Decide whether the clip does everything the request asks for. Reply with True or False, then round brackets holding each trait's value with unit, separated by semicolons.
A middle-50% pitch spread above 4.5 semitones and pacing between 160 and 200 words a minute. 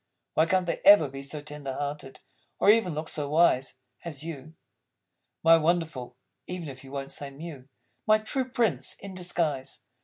False (4.2 semitones; 165 wpm)